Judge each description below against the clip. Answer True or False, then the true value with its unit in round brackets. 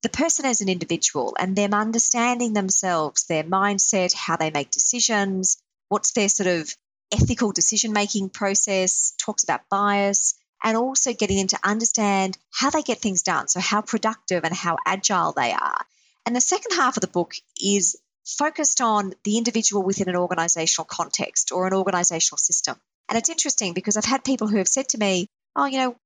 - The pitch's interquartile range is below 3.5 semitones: False (3.9 semitones)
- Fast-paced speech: False (185 wpm)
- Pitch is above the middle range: True (205 Hz)